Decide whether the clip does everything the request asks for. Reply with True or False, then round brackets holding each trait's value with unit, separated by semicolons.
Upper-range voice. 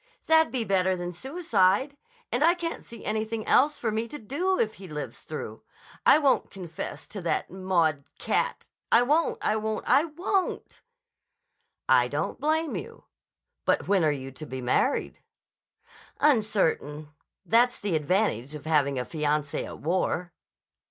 True (205 Hz)